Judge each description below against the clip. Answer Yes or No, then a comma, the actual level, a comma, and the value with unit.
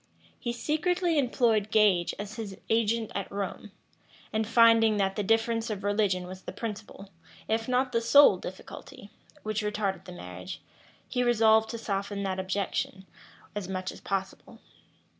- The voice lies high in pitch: Yes, high, 210 Hz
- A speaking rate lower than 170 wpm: Yes, average, 150 wpm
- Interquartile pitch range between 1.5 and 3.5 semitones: Yes, average, 2.9 semitones